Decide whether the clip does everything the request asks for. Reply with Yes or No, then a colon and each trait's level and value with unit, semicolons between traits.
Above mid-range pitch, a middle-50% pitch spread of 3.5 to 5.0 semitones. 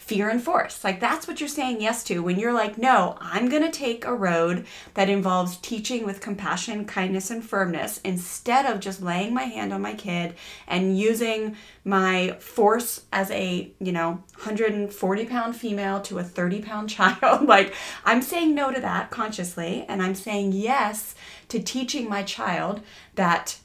Yes: high, 205 Hz; average, 3.8 semitones